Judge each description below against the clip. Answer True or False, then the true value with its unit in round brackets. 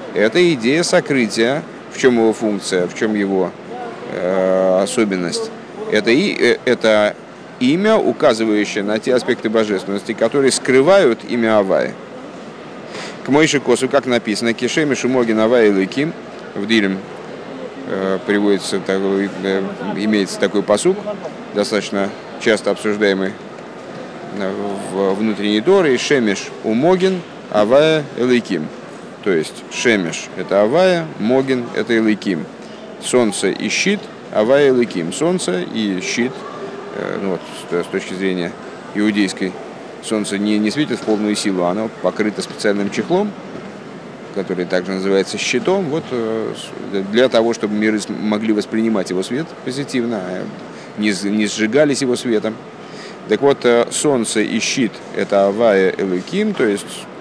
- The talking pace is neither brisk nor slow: True (120 wpm)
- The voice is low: True (110 Hz)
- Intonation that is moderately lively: True (4.5 semitones)